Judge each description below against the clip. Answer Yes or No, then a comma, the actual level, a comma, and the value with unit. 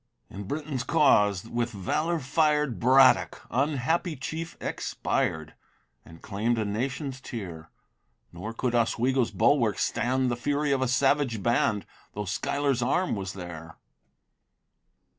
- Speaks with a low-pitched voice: Yes, low, 125 Hz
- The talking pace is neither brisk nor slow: No, slow, 120 wpm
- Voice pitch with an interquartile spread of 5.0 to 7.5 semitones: Yes, average, 5.3 semitones